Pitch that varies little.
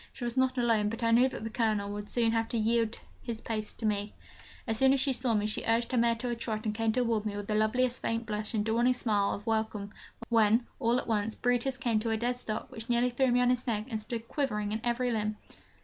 Yes: narrow, 2.1 semitones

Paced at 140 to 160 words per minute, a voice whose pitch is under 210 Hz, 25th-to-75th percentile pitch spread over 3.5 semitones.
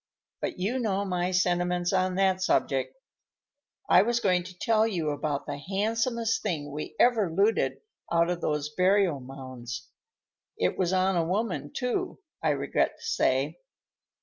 Yes: average, 150 wpm; medium, 185 Hz; average, 4.3 semitones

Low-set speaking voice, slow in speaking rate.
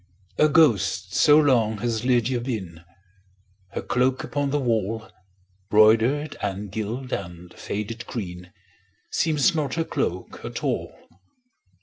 Yes: low, 115 Hz; slow, 120 wpm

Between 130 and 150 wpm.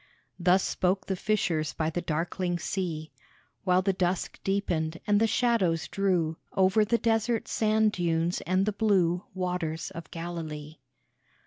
Yes: average, 140 wpm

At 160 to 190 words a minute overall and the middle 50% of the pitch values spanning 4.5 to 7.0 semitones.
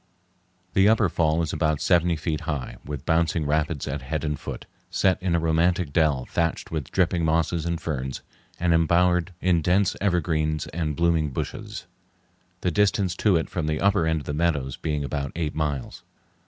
No: average, 180 wpm; narrow, 2.4 semitones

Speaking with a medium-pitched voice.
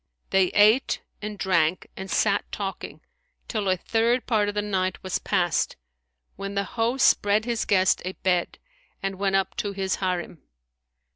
No: high, 195 Hz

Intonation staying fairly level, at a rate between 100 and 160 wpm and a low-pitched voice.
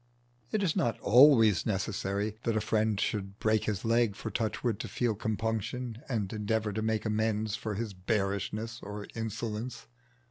Yes: narrow, 1.8 semitones; average, 155 wpm; low, 110 Hz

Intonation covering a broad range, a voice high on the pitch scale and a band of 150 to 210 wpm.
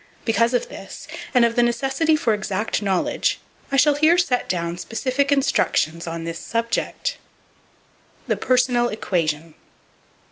No: wide, 6.5 semitones; high, 235 Hz; slow, 135 wpm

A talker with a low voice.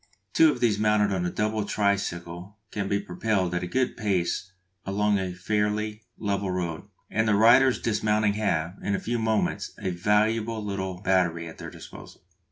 Yes: low, 100 Hz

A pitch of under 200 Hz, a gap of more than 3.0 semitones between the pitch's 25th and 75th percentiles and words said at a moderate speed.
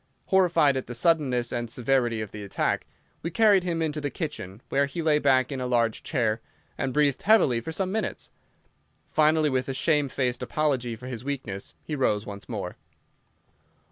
Yes: low, 135 Hz; average, 4.4 semitones; average, 175 wpm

